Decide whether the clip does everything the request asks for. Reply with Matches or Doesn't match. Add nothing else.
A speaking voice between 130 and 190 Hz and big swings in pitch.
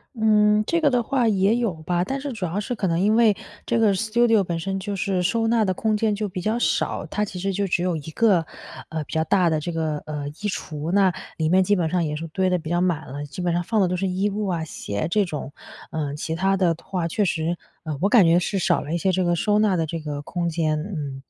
Doesn't match